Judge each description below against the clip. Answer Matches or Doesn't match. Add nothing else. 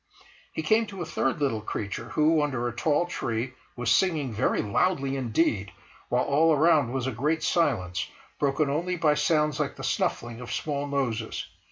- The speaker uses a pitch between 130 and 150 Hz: Matches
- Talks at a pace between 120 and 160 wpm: Doesn't match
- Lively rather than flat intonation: Doesn't match